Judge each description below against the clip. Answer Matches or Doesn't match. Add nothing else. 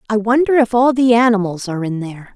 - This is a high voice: Matches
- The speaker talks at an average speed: Doesn't match